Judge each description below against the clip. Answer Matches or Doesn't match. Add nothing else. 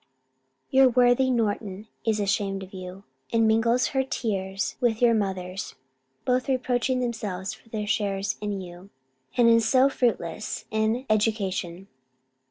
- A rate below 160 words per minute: Matches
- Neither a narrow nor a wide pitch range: Matches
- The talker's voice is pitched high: Matches